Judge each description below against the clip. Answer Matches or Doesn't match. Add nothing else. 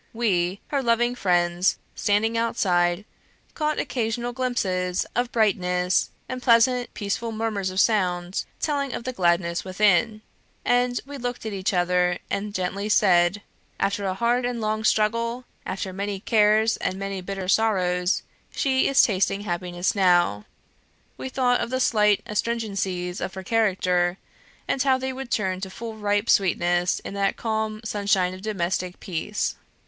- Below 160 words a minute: Matches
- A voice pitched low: Doesn't match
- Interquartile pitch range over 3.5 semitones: Matches